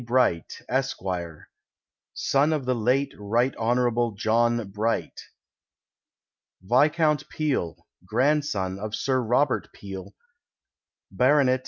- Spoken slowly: Yes, slow, 90 wpm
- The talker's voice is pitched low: Yes, low, 120 Hz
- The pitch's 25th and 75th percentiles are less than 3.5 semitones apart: No, average, 4.1 semitones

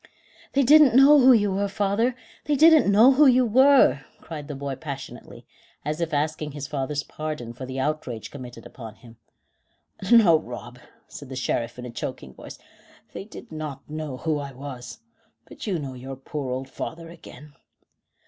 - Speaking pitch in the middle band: Yes, medium, 150 Hz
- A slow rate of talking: No, average, 175 wpm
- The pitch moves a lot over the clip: Yes, wide, 7.6 semitones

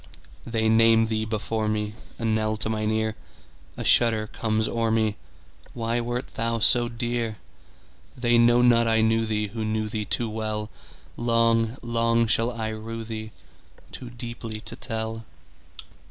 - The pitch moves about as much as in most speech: No, narrow, 1.2 semitones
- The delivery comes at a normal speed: No, slow, 125 wpm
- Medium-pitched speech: No, low, 115 Hz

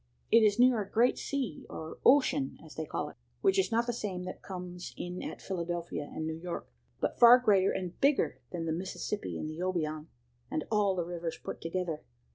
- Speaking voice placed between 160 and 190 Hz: Yes, medium, 185 Hz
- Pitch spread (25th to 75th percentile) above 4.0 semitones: Yes, average, 5.2 semitones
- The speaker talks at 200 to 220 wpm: Yes, fast, 205 wpm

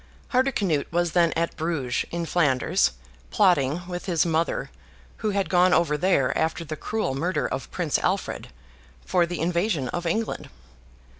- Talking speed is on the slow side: No, average, 150 wpm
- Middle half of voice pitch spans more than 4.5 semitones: No, narrow, 2.6 semitones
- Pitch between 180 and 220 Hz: No, medium, 170 Hz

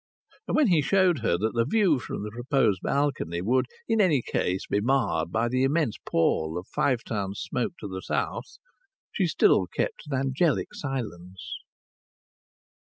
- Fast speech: No, average, 165 wpm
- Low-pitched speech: Yes, low, 125 Hz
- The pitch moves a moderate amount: No, wide, 6.7 semitones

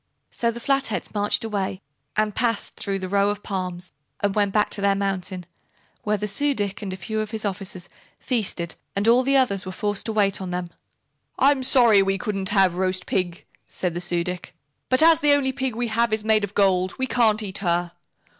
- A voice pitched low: No, high, 205 Hz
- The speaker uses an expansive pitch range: No, average, 3.2 semitones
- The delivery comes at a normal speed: No, fast, 210 wpm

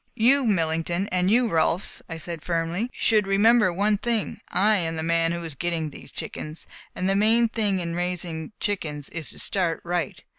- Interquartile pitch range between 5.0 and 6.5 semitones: No, average, 4.0 semitones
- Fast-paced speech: No, average, 185 wpm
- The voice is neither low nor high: Yes, medium, 180 Hz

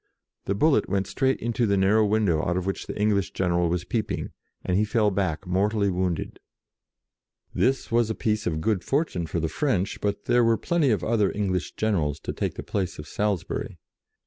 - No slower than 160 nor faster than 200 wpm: Yes, average, 195 wpm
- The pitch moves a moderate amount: Yes, average, 3.5 semitones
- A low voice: Yes, low, 100 Hz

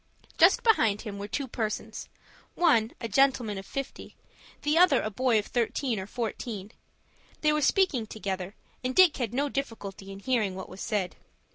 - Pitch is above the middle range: Yes, high, 225 Hz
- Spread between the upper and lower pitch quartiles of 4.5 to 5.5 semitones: Yes, average, 5.2 semitones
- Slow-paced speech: No, average, 165 wpm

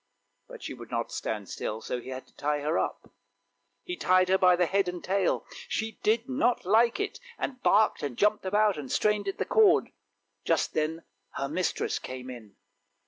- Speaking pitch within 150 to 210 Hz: Yes, medium, 185 Hz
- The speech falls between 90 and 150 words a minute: No, average, 195 wpm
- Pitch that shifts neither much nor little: No, wide, 6.6 semitones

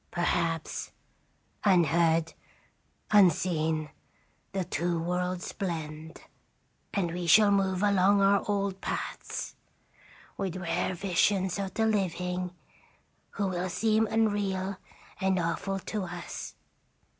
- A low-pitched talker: No, medium, 185 Hz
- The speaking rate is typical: No, slow, 100 wpm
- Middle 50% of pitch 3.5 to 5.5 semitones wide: No, narrow, 2.6 semitones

